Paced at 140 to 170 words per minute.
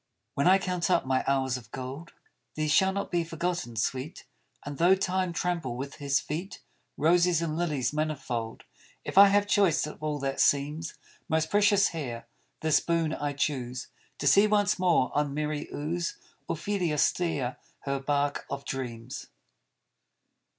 Yes: average, 155 wpm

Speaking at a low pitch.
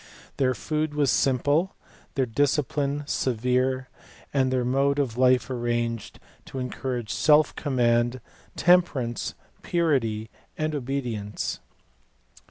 Yes: low, 130 Hz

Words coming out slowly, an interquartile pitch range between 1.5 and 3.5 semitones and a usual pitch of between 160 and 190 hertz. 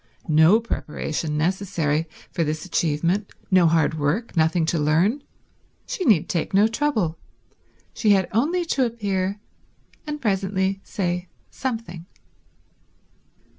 No: slow, 115 wpm; average, 5.1 semitones; medium, 185 Hz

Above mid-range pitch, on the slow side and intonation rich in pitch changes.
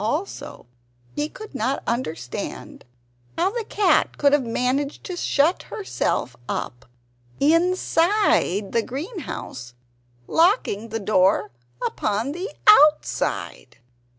Yes: very high, 285 Hz; slow, 100 wpm; wide, 8.7 semitones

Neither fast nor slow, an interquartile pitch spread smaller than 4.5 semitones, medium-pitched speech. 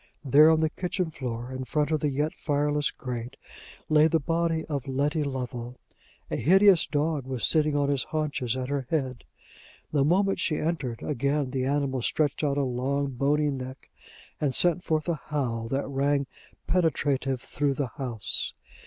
Yes: average, 170 wpm; average, 2.9 semitones; medium, 145 Hz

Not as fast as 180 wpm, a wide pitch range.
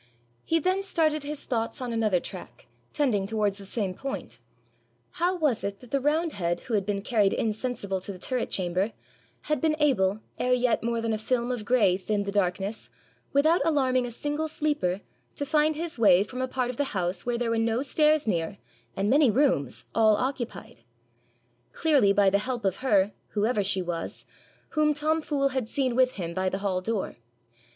No: average, 190 wpm; wide, 6.0 semitones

